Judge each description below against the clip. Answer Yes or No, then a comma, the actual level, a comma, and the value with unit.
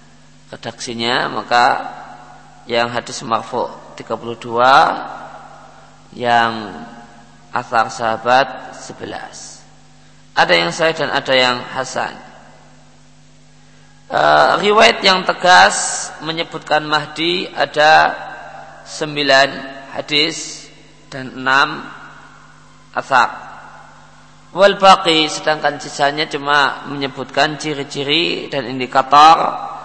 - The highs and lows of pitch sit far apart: No, average, 4.4 semitones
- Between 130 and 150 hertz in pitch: Yes, low, 135 Hz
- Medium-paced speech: No, slow, 75 wpm